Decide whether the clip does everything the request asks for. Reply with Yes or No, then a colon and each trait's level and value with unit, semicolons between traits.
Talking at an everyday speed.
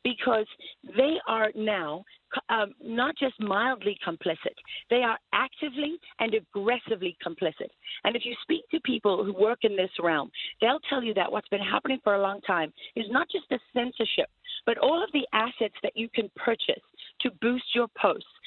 Yes: average, 180 wpm